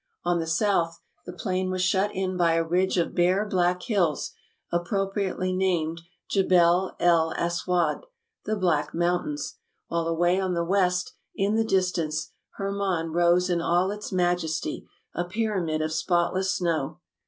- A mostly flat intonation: Yes, narrow, 2.0 semitones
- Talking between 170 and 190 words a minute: No, average, 150 wpm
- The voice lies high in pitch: No, medium, 180 Hz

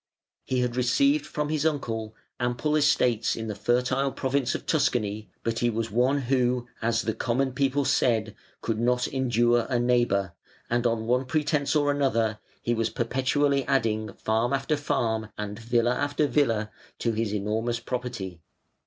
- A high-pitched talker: No, low, 120 Hz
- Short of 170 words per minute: Yes, average, 160 wpm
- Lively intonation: No, average, 3.2 semitones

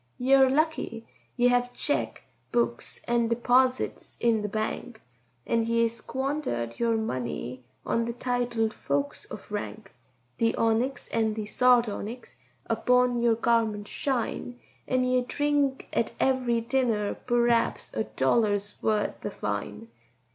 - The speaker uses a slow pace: Yes, slow, 125 wpm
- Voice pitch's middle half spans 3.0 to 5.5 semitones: No, narrow, 2.5 semitones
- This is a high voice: Yes, high, 235 Hz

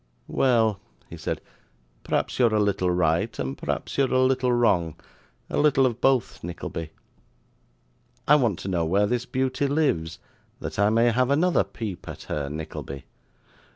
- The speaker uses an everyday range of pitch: No, wide, 6.9 semitones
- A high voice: No, low, 110 Hz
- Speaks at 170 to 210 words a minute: No, average, 155 wpm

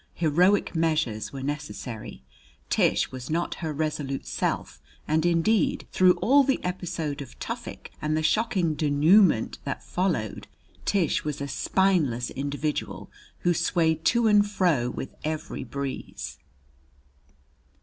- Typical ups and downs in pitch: Yes, average, 4.5 semitones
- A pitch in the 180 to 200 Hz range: No, medium, 155 Hz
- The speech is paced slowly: Yes, slow, 125 wpm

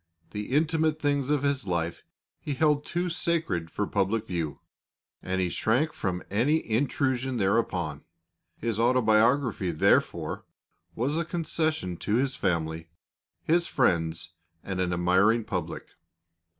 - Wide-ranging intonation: Yes, wide, 8.0 semitones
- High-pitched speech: No, low, 115 Hz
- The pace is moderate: No, slow, 125 wpm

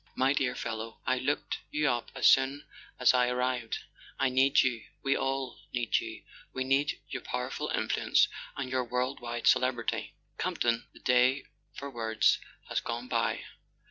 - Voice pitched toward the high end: No, low, 125 Hz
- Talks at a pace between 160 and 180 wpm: Yes, average, 165 wpm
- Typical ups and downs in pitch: No, narrow, 1.8 semitones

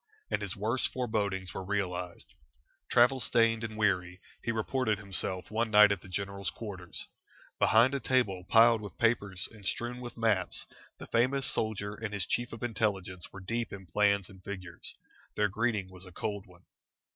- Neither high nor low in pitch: No, low, 105 Hz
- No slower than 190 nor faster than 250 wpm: No, average, 170 wpm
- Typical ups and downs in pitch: Yes, average, 3.3 semitones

